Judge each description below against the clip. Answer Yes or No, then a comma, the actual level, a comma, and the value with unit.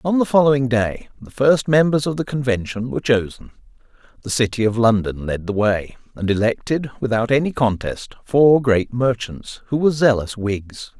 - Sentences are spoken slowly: No, average, 170 wpm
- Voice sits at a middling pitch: No, low, 120 Hz